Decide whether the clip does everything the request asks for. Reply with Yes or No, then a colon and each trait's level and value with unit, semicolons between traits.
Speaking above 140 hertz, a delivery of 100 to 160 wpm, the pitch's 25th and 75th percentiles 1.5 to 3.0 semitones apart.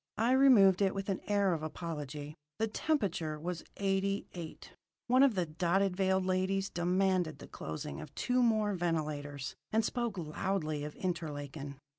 No: medium, 185 Hz; average, 155 wpm; average, 4.2 semitones